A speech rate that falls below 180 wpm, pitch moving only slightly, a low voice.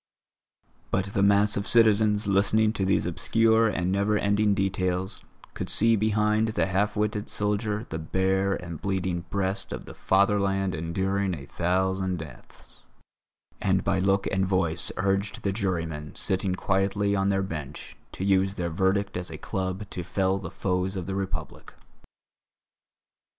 Yes: average, 150 wpm; narrow, 1.7 semitones; very low, 95 Hz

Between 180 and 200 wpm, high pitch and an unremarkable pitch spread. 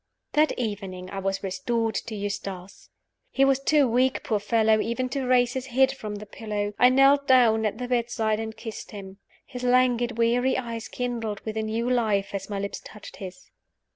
Yes: average, 190 wpm; high, 230 Hz; average, 3.4 semitones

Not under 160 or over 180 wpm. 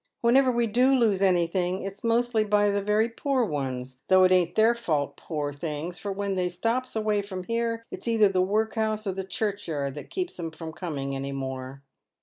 No: average, 195 wpm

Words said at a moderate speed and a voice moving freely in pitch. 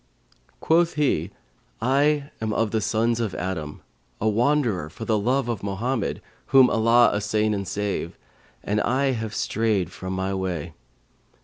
No: average, 145 wpm; average, 3.9 semitones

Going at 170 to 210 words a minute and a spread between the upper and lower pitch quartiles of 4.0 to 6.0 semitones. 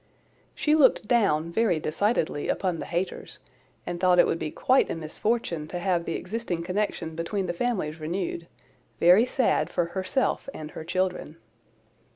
No: average, 155 wpm; average, 4.3 semitones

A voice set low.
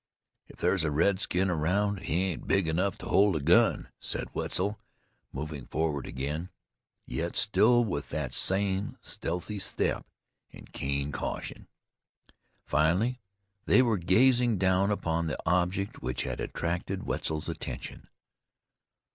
Yes: very low, 90 Hz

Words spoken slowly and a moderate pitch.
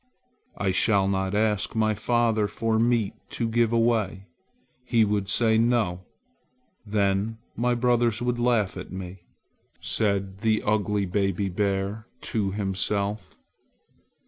No: slow, 120 wpm; low, 105 Hz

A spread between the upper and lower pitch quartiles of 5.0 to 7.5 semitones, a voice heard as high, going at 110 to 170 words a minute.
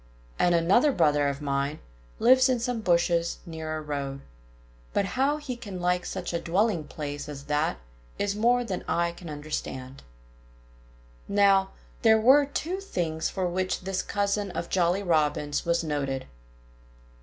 No: wide, 5.5 semitones; medium, 175 Hz; average, 150 wpm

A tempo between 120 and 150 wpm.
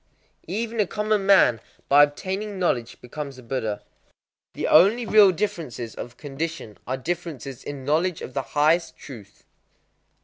Yes: average, 145 wpm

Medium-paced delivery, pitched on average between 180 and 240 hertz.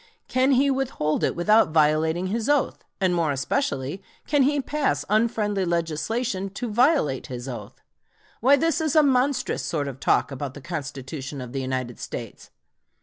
Yes: average, 160 wpm; medium, 185 Hz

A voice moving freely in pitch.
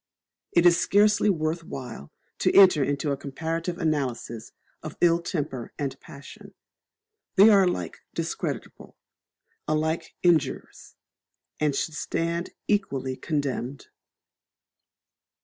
No: average, 3.8 semitones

